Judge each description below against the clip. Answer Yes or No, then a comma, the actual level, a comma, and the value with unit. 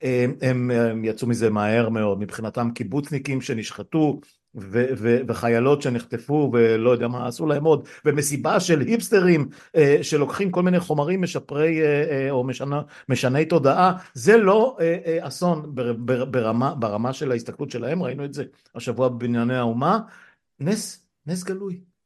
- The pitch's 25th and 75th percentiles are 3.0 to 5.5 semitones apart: Yes, average, 4.9 semitones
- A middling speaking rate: Yes, average, 125 wpm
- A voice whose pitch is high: No, medium, 140 Hz